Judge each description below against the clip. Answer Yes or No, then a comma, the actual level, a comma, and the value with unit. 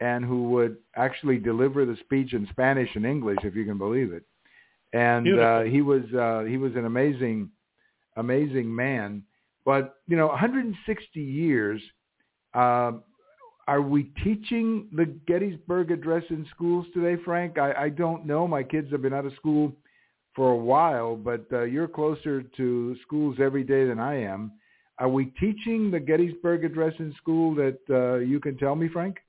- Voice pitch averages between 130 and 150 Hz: Yes, medium, 140 Hz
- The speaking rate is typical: Yes, average, 170 wpm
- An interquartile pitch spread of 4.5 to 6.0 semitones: Yes, average, 4.9 semitones